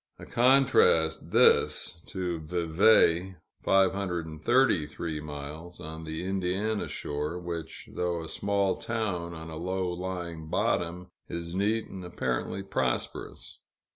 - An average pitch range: Yes, average, 3.1 semitones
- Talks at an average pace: No, slow, 110 wpm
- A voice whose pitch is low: Yes, very low, 90 Hz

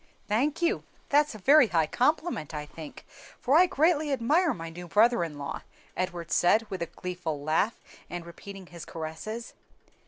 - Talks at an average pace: Yes, average, 165 wpm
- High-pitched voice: Yes, high, 195 Hz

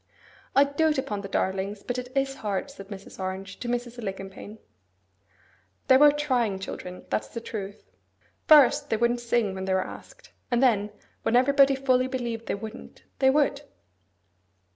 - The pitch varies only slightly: No, average, 5.2 semitones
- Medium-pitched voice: No, high, 240 Hz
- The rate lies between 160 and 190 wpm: Yes, average, 165 wpm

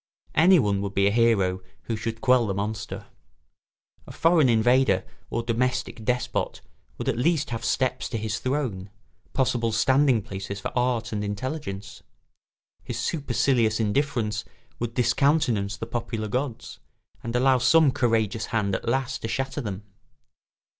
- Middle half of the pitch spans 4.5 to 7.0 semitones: No, average, 3.5 semitones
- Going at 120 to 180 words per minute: Yes, average, 140 wpm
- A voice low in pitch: Yes, low, 115 Hz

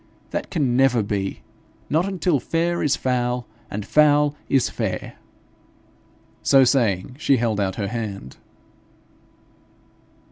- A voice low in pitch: Yes, low, 125 Hz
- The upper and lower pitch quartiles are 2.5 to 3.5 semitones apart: No, wide, 5.6 semitones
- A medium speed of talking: No, slow, 115 wpm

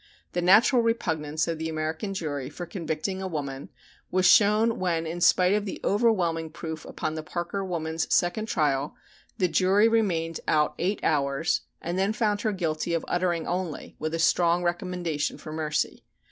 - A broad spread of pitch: No, average, 3.2 semitones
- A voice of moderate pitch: Yes, medium, 170 Hz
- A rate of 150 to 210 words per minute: Yes, average, 170 wpm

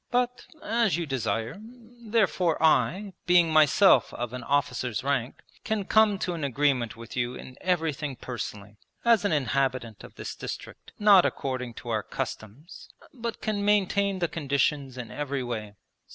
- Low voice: No, medium, 145 Hz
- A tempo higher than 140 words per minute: Yes, average, 150 wpm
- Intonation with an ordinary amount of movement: No, wide, 8.0 semitones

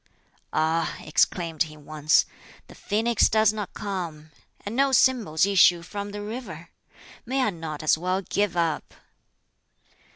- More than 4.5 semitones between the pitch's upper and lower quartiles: Yes, average, 4.9 semitones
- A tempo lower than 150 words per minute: Yes, slow, 135 wpm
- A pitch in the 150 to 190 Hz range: Yes, medium, 185 Hz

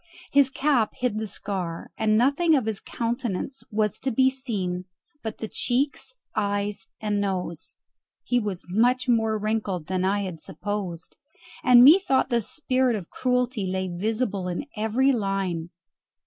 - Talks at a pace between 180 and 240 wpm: No, average, 150 wpm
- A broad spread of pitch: No, average, 4.4 semitones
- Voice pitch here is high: Yes, high, 215 Hz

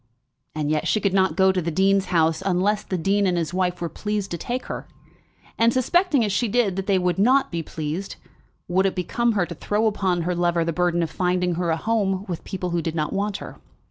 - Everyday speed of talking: No, fast, 240 wpm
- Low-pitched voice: No, medium, 185 Hz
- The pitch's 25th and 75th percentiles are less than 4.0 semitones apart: Yes, average, 2.9 semitones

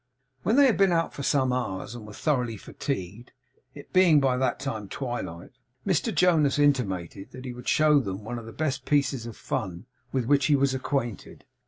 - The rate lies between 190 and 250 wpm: Yes, average, 195 wpm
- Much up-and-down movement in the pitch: No, average, 4.3 semitones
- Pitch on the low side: Yes, low, 130 Hz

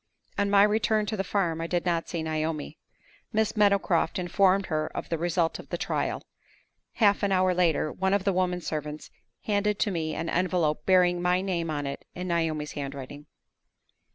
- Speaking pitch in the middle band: Yes, medium, 180 Hz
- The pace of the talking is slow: No, average, 180 wpm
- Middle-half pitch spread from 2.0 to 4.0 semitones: Yes, average, 3.7 semitones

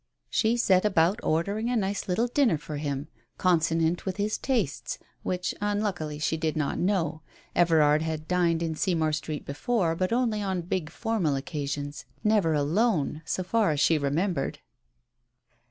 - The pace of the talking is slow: No, average, 155 wpm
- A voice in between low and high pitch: Yes, medium, 170 Hz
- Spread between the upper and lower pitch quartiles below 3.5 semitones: No, average, 4.8 semitones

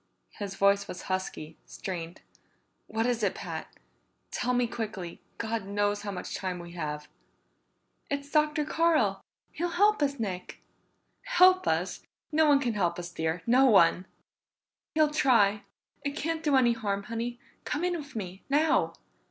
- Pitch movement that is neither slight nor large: No, wide, 7.5 semitones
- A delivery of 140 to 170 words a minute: Yes, average, 150 wpm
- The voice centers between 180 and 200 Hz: No, high, 225 Hz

